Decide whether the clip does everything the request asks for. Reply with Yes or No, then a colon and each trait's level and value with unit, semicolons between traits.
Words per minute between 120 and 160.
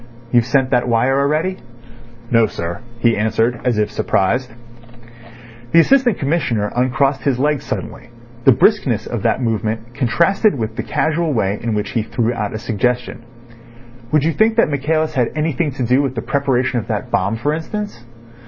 No: average, 170 wpm